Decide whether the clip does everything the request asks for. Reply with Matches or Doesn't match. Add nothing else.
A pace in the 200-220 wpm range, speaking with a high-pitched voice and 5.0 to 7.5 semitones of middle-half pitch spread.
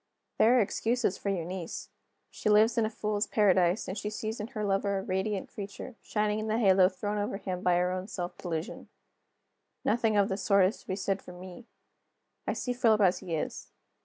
Doesn't match